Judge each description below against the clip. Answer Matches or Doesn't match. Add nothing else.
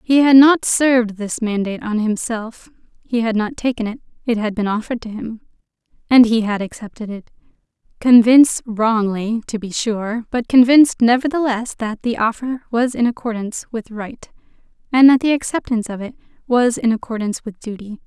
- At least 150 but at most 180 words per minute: Matches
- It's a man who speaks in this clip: Doesn't match